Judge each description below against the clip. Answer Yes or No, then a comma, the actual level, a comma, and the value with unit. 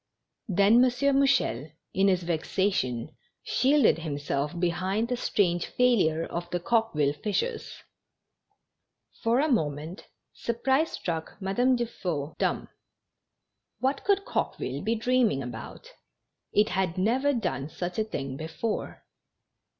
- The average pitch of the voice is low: No, high, 190 Hz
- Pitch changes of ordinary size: No, wide, 7.3 semitones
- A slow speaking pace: Yes, slow, 115 wpm